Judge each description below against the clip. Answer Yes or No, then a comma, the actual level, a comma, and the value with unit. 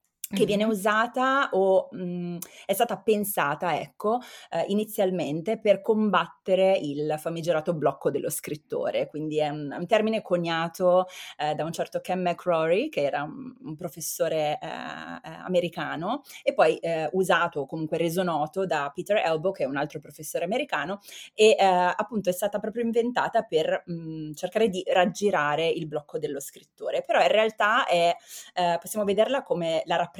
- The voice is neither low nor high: Yes, medium, 180 Hz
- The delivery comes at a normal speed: Yes, average, 160 wpm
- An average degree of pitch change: Yes, average, 4.4 semitones